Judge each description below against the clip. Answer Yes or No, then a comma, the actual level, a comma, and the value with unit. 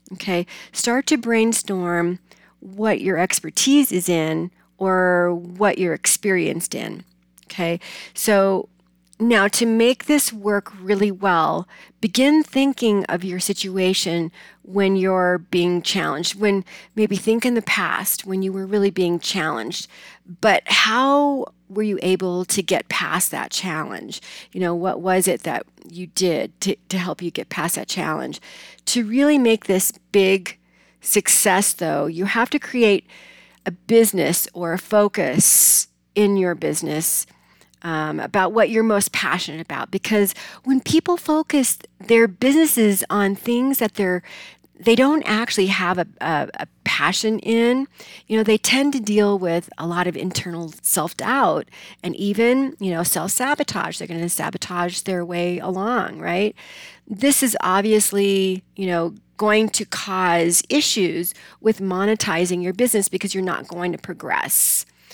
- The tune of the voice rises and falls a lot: No, average, 3.7 semitones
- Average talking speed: Yes, average, 150 wpm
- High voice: Yes, high, 195 Hz